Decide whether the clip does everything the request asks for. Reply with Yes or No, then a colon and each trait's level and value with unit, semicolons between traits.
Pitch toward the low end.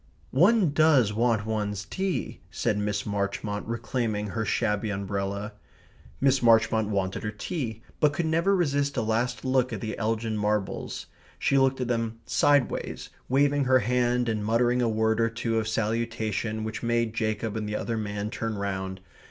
Yes: low, 115 Hz